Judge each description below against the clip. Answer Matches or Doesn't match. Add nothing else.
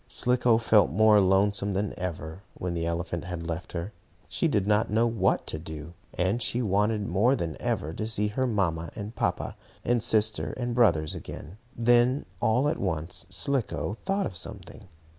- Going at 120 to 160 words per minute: Doesn't match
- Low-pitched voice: Matches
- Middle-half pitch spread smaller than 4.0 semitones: Doesn't match